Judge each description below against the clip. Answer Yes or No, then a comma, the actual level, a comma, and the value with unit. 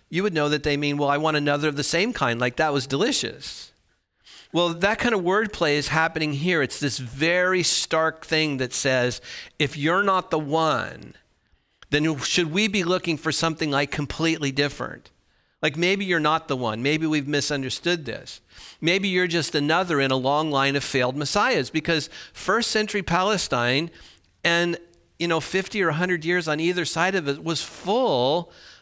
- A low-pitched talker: No, medium, 160 Hz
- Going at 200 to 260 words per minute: No, average, 180 wpm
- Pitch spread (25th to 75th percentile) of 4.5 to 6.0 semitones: No, average, 3.4 semitones